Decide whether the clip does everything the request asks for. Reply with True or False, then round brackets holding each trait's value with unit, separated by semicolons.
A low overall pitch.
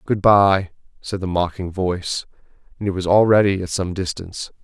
True (95 Hz)